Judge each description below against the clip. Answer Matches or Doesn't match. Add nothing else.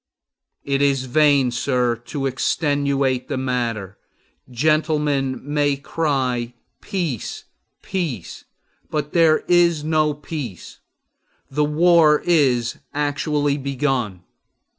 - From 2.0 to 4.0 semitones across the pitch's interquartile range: Matches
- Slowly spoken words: Matches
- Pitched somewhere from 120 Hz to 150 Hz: Matches